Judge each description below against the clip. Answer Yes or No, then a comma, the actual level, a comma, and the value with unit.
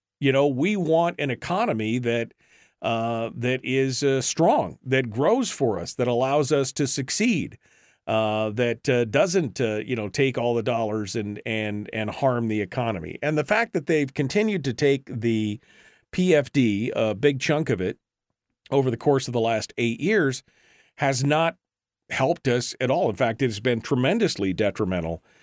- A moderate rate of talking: Yes, average, 175 wpm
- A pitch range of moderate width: Yes, average, 4.1 semitones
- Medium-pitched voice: No, low, 130 Hz